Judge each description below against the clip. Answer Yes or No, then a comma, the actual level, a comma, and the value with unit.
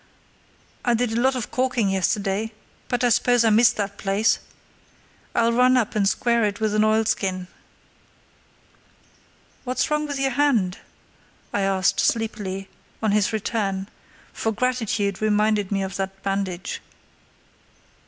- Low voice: No, high, 215 Hz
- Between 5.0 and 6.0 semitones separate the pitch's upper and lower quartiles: No, average, 3.3 semitones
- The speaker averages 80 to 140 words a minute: Yes, slow, 135 wpm